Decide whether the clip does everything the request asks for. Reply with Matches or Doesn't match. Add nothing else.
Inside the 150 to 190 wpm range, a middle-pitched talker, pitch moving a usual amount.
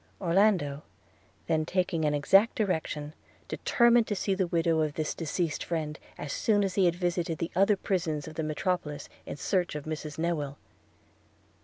Matches